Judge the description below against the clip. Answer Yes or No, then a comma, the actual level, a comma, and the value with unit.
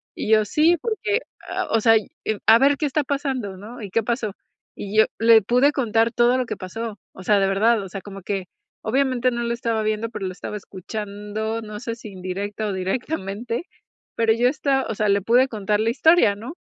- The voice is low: No, high, 225 Hz